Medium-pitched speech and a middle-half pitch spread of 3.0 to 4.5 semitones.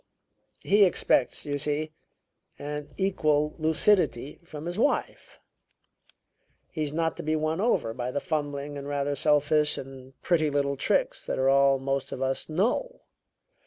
No: medium, 150 Hz; narrow, 2.6 semitones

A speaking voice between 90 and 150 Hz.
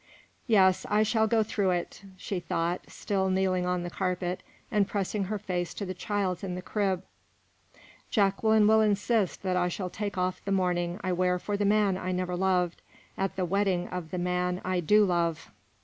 No: medium, 185 Hz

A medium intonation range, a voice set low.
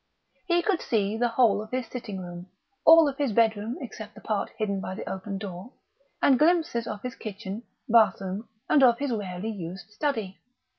No: average, 4.2 semitones; high, 220 Hz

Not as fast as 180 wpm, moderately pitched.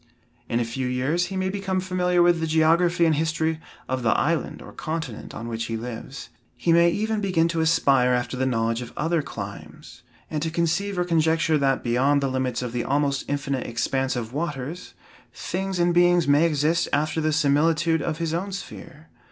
No: average, 195 wpm; medium, 155 Hz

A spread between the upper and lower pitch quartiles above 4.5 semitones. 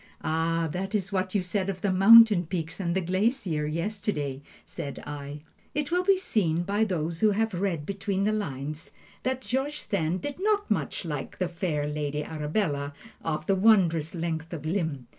Yes: average, 4.9 semitones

